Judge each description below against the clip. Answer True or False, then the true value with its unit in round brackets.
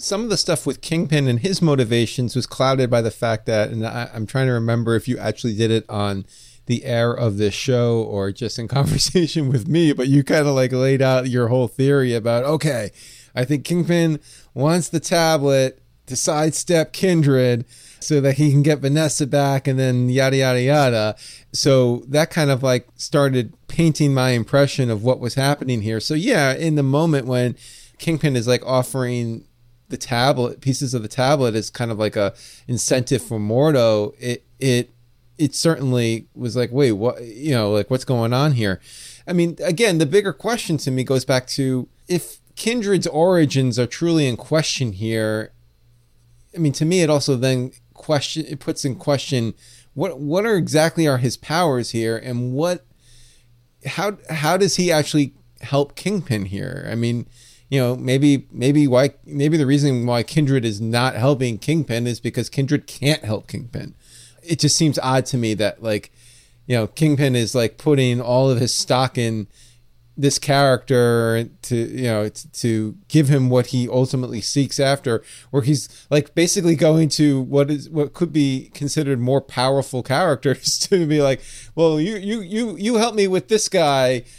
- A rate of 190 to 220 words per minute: False (180 wpm)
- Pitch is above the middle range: False (130 Hz)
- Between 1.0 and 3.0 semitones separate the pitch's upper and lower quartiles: False (3.9 semitones)